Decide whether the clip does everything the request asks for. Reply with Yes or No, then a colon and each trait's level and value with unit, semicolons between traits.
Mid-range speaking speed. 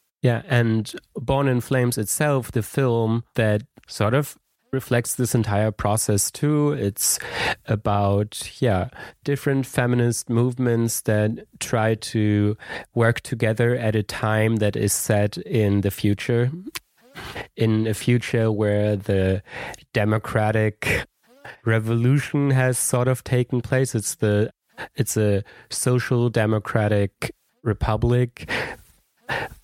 No: slow, 110 wpm